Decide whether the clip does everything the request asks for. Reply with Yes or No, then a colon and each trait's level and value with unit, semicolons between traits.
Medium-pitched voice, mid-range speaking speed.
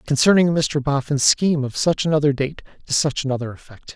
Yes: medium, 145 Hz; average, 180 wpm